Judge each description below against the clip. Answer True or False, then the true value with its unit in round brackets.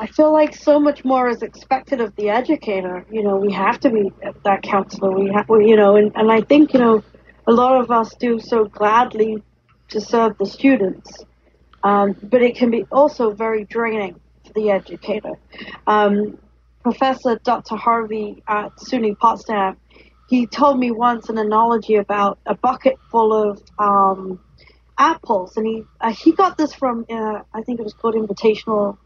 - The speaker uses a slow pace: False (175 wpm)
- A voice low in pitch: False (220 Hz)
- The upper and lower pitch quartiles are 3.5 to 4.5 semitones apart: False (2.8 semitones)